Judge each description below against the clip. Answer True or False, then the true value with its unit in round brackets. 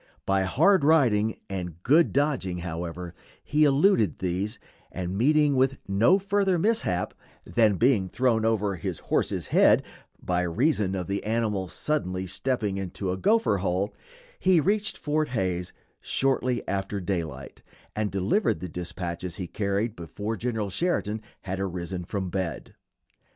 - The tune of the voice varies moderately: False (6.5 semitones)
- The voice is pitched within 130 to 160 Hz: False (100 Hz)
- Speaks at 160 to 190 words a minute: False (140 wpm)